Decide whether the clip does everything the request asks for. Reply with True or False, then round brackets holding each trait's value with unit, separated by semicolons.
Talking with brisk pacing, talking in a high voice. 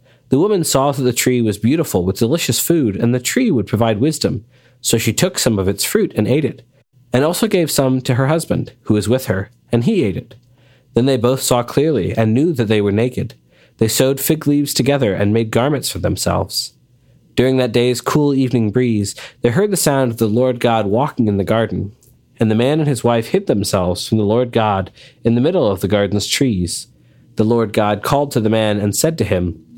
False (225 wpm; 120 Hz)